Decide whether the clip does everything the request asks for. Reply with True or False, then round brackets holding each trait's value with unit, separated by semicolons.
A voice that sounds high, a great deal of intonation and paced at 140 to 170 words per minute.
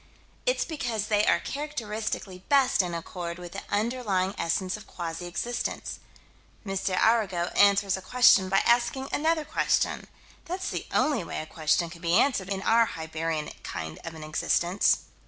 True (195 Hz; 5.7 semitones; 155 wpm)